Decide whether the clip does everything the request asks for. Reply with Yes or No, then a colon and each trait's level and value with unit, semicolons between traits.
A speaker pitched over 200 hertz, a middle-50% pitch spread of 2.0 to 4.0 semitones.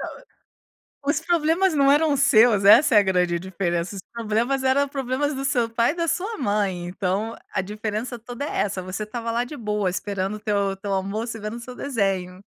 No: high, 220 Hz; wide, 5.6 semitones